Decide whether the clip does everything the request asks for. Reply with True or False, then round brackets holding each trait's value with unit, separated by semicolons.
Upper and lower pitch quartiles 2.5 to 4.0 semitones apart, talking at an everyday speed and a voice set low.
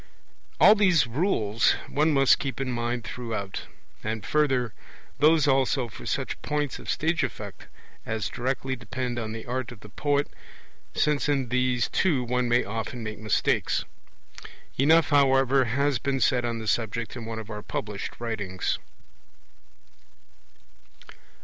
True (3.6 semitones; 145 wpm; 125 Hz)